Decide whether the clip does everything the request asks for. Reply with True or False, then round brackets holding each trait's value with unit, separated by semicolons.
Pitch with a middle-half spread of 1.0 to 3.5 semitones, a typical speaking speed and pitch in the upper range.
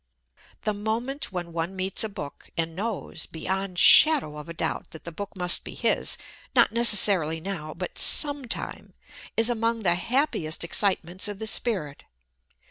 False (5.0 semitones; 155 wpm; 195 Hz)